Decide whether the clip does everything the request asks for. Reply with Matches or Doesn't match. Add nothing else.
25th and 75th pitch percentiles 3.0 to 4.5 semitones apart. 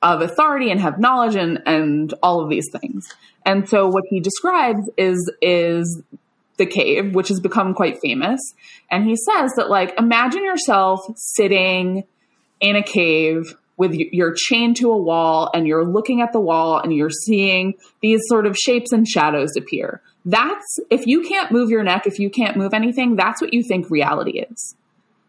Doesn't match